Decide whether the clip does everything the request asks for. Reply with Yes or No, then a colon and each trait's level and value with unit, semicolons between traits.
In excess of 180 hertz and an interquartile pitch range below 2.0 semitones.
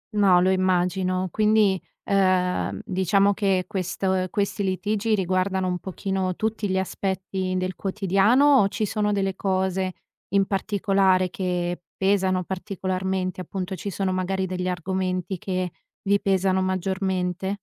Yes: high, 190 Hz; narrow, 1.2 semitones